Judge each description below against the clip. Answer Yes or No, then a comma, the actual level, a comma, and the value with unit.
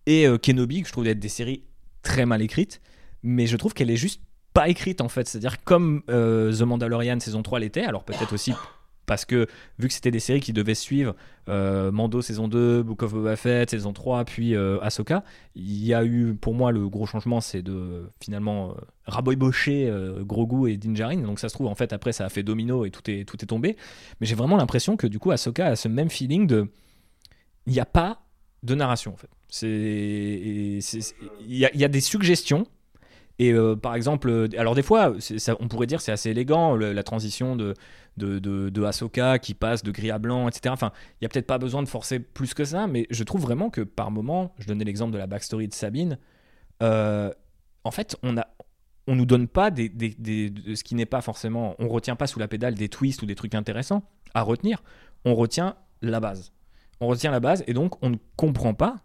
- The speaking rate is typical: No, fast, 230 wpm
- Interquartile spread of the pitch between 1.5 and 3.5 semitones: Yes, average, 3.2 semitones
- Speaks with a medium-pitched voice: No, low, 115 Hz